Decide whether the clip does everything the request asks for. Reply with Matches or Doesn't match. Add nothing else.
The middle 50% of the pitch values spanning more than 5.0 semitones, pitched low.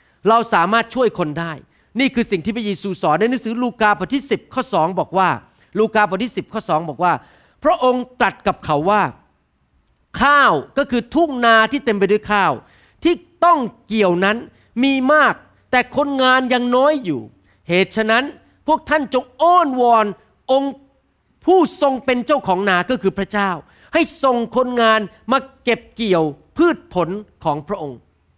Doesn't match